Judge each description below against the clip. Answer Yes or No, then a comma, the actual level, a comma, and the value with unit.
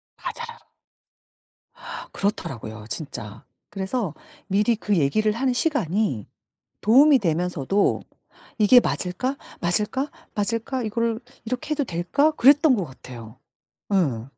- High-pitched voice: Yes, high, 210 Hz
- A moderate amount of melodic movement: No, wide, 7.2 semitones